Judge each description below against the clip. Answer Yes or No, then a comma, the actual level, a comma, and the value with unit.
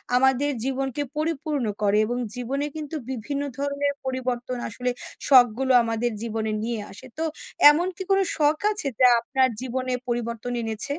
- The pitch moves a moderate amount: Yes, average, 3.1 semitones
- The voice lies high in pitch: Yes, very high, 260 Hz